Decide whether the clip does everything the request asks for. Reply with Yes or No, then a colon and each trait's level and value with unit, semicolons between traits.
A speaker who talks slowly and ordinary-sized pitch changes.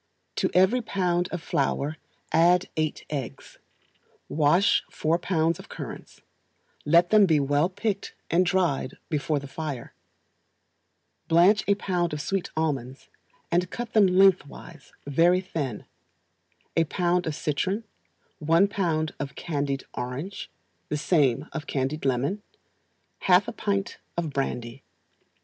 Yes: slow, 125 wpm; average, 4.3 semitones